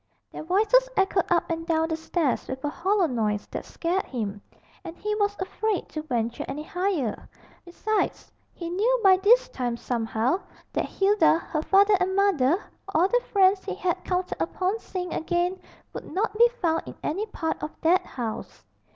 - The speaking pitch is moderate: No, very high, 360 Hz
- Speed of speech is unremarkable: Yes, average, 175 wpm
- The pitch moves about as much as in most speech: Yes, average, 4.4 semitones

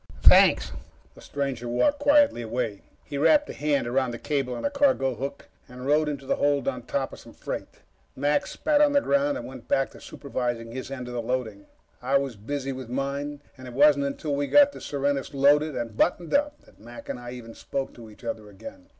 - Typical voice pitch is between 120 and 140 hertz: Yes, low, 135 Hz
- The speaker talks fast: Yes, fast, 220 wpm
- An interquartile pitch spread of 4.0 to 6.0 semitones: No, average, 3.4 semitones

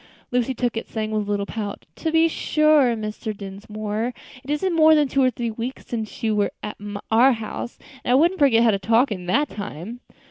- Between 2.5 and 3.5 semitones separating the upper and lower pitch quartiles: No, average, 4.2 semitones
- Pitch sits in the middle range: No, high, 230 Hz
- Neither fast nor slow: No, fast, 215 wpm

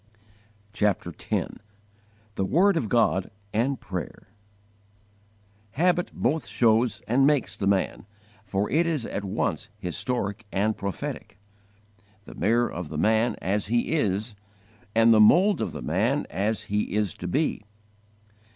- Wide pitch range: No, average, 4.6 semitones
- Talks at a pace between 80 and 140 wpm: Yes, slow, 135 wpm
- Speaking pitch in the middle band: No, low, 110 Hz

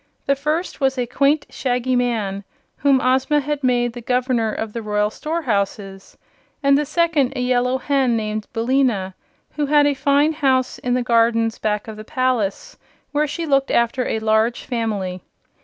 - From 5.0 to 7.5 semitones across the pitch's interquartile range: No, average, 3.9 semitones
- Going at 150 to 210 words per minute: Yes, average, 170 wpm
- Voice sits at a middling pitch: No, very high, 250 Hz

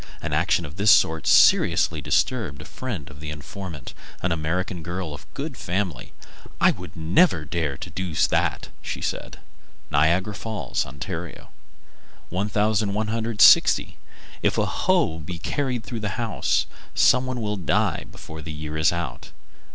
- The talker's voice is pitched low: Yes, very low, 90 Hz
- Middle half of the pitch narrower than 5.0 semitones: No, wide, 5.4 semitones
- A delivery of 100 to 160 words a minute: Yes, average, 145 wpm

